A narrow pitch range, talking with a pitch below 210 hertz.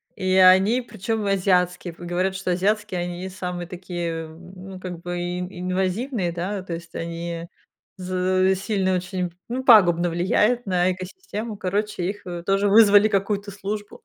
Yes: narrow, 2.3 semitones; medium, 185 Hz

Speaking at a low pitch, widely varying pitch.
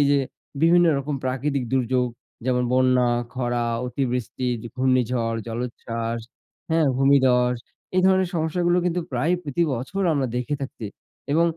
No: low, 130 Hz; average, 3.4 semitones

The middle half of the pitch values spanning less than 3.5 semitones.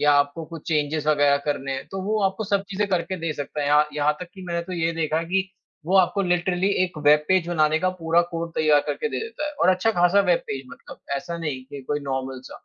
No: average, 3.9 semitones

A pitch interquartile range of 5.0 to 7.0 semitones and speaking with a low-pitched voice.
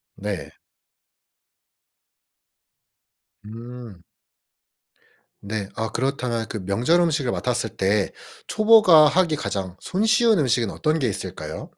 No: wide, 7.5 semitones; low, 120 Hz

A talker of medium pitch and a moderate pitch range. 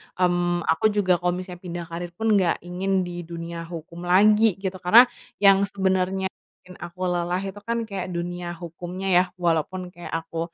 No: medium, 180 Hz; narrow, 1.7 semitones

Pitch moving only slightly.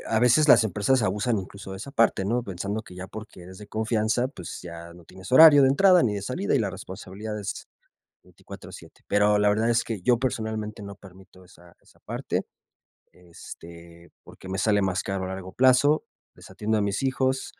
No: average, 4.2 semitones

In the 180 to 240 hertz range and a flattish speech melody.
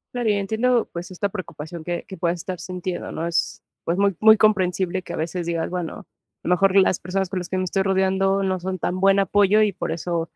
Yes: medium, 185 Hz; narrow, 2.0 semitones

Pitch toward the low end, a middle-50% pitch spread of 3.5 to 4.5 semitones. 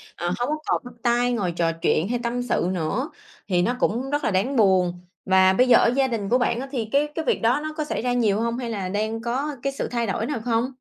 No: high, 235 Hz; average, 4.1 semitones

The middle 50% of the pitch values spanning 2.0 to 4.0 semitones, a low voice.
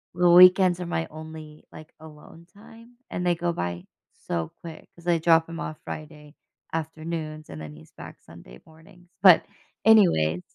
No: average, 2.7 semitones; medium, 160 Hz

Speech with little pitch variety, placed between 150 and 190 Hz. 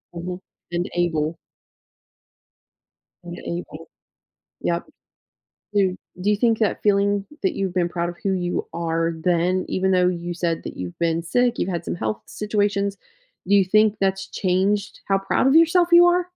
No: average, 3.0 semitones; medium, 185 Hz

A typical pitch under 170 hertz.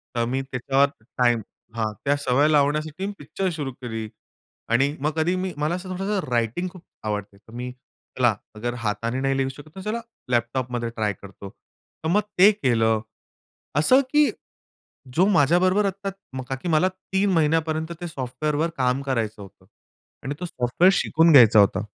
Yes: medium, 140 Hz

